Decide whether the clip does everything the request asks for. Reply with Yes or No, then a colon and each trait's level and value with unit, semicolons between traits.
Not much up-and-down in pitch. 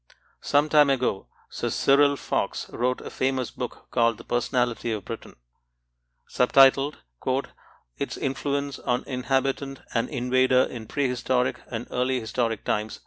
Yes: narrow, 2.0 semitones